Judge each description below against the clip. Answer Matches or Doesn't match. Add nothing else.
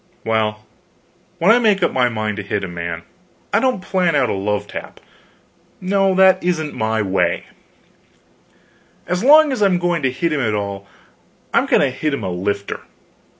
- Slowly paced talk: Doesn't match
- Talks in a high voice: Doesn't match